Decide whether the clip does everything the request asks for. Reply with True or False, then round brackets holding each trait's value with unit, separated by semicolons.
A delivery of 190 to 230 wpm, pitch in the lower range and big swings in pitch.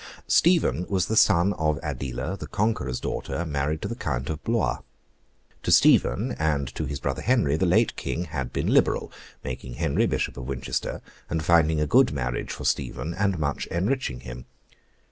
False (175 wpm; 80 Hz; 6.0 semitones)